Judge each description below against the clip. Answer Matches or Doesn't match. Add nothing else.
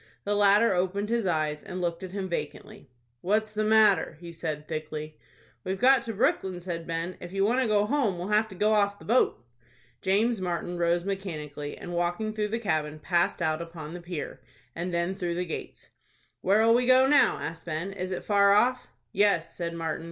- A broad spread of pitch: Doesn't match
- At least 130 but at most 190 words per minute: Doesn't match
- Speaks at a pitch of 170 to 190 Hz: Matches